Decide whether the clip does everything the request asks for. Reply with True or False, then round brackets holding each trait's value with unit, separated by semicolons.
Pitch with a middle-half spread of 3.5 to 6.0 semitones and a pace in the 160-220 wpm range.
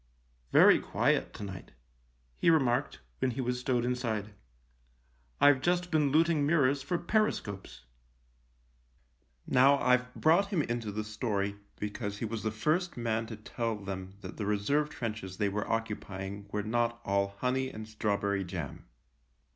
True (4.7 semitones; 165 wpm)